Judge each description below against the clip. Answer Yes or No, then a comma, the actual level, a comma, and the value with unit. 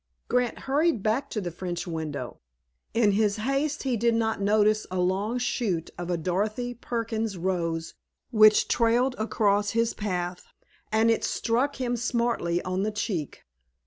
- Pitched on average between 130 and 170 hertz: No, high, 215 Hz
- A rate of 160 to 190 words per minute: No, average, 150 wpm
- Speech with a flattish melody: No, average, 4.5 semitones